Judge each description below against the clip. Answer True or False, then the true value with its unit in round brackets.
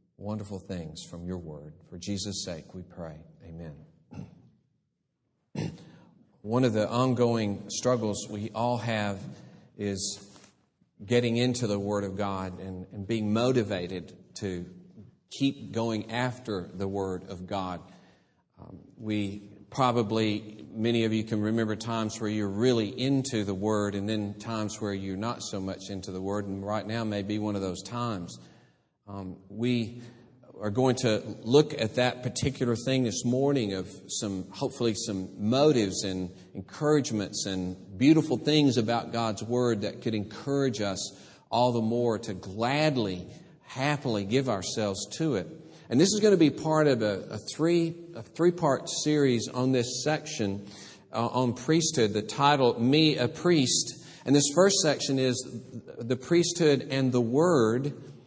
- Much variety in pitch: False (4.1 semitones)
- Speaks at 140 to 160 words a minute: True (150 wpm)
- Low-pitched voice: True (110 Hz)